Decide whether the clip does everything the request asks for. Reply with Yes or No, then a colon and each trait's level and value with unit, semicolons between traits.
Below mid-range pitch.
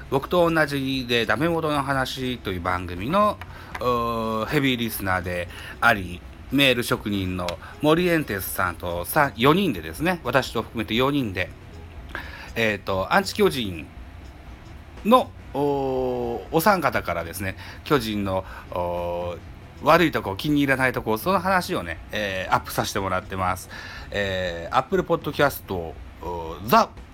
Yes: low, 110 Hz